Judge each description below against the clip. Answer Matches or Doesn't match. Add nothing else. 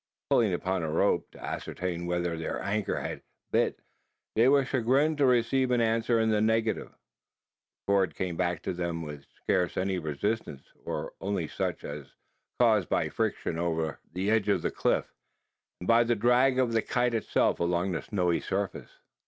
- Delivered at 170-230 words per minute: Matches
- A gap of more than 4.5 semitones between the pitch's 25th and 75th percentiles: Matches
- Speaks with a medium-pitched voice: Doesn't match